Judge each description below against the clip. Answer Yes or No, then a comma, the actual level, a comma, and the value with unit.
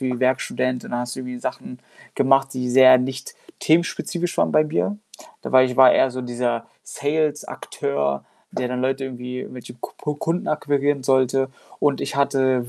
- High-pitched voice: No, low, 130 Hz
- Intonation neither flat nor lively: No, narrow, 1.9 semitones